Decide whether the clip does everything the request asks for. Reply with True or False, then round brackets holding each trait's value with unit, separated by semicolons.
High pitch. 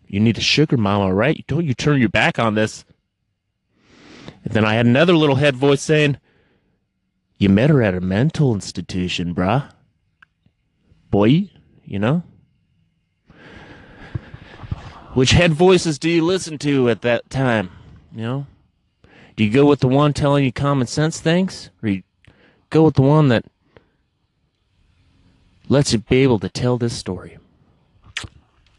False (120 Hz)